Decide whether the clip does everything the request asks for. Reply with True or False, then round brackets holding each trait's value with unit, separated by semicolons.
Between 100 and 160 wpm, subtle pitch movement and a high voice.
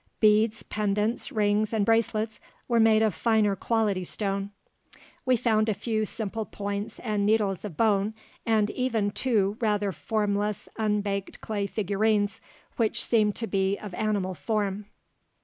True (140 wpm; 1.5 semitones; 210 Hz)